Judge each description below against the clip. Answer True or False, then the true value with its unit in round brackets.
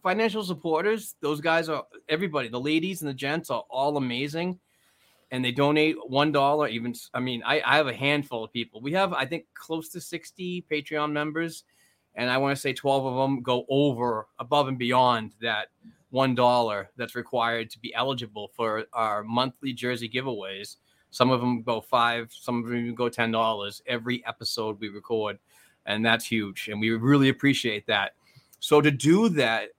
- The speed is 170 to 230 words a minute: True (185 wpm)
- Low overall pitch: True (130 Hz)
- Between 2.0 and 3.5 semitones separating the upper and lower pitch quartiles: False (4.2 semitones)